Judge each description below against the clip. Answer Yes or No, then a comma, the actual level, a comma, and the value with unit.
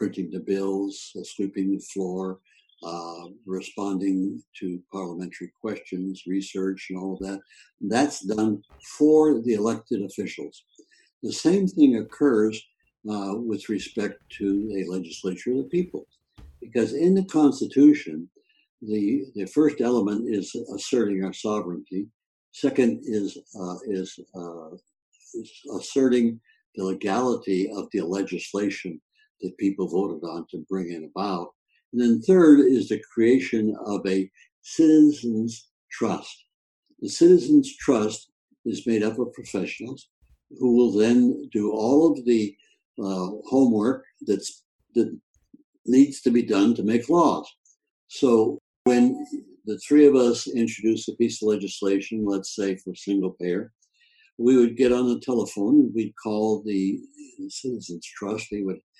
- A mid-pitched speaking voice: No, low, 110 Hz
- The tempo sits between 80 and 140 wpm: Yes, slow, 135 wpm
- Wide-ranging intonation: Yes, wide, 6.6 semitones